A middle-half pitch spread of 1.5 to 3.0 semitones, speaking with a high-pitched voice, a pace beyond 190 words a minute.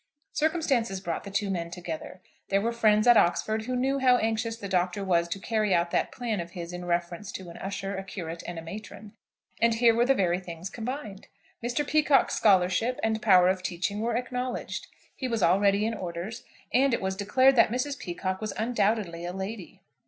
No: average, 4.5 semitones; high, 205 Hz; average, 200 wpm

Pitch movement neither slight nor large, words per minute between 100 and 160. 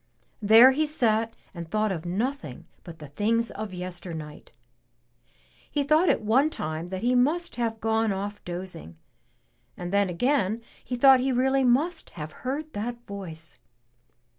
No: wide, 6.3 semitones; average, 150 wpm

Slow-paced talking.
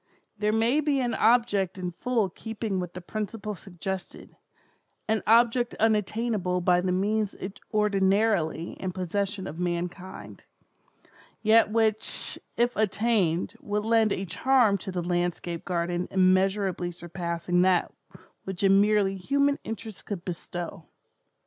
Yes: slow, 125 wpm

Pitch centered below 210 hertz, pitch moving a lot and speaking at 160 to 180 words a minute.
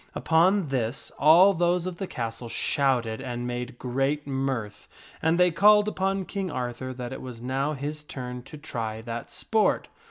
Yes: low, 135 Hz; wide, 5.8 semitones; average, 165 wpm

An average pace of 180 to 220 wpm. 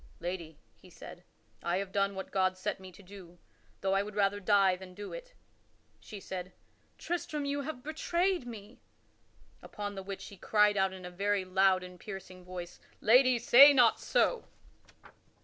No: average, 170 wpm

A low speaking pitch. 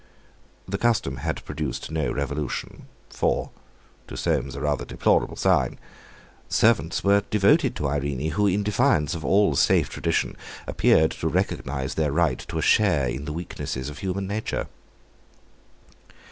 Yes: very low, 80 Hz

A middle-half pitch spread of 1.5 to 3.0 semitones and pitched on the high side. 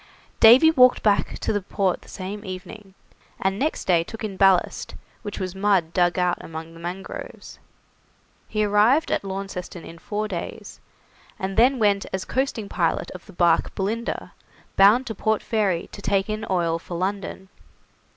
Yes: average, 2.7 semitones; high, 195 Hz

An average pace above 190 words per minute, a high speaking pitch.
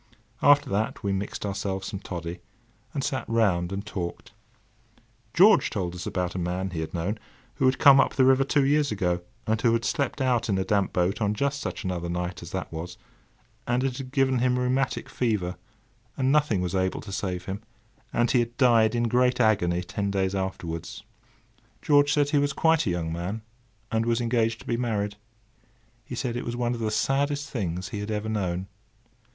No: average, 200 wpm; low, 110 Hz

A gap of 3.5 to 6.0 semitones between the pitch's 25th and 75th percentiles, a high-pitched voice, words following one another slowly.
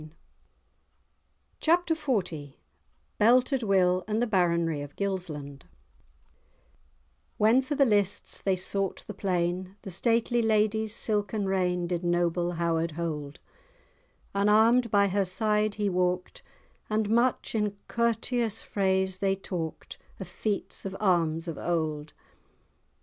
Yes: average, 3.9 semitones; high, 195 Hz; slow, 120 wpm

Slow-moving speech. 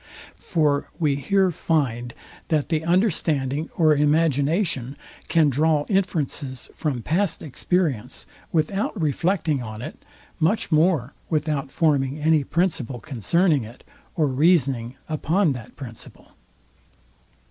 Yes: slow, 110 wpm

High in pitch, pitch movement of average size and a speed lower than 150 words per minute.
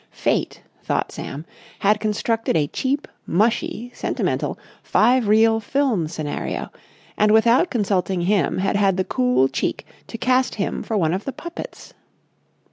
Yes: high, 215 Hz; average, 4.3 semitones; average, 140 wpm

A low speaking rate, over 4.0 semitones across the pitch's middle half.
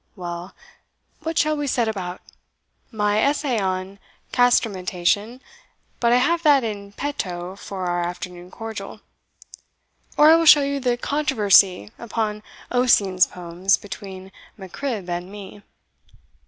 Yes: slow, 125 wpm; average, 5.3 semitones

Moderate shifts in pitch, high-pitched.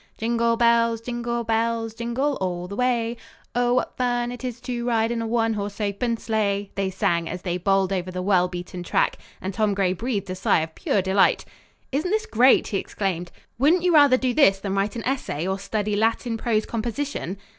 Yes: average, 3.7 semitones; high, 225 Hz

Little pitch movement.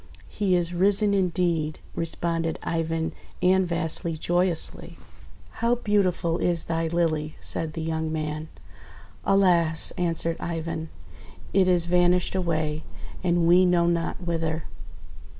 Yes: narrow, 1.8 semitones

